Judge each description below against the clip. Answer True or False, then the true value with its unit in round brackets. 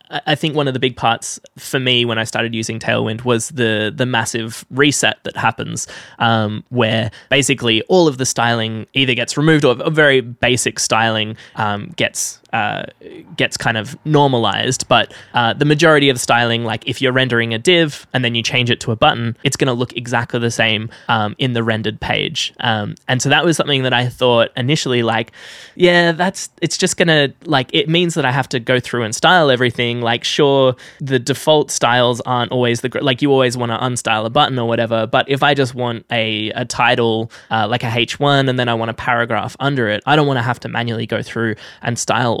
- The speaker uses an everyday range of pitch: True (3.3 semitones)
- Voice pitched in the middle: False (125 Hz)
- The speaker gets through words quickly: True (220 wpm)